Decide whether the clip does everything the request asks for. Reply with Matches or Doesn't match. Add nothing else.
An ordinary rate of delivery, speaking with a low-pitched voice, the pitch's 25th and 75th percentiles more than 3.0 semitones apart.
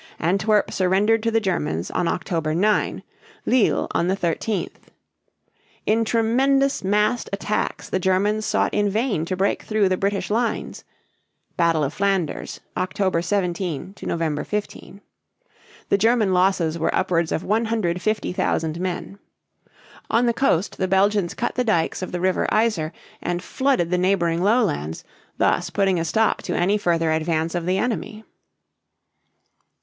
Doesn't match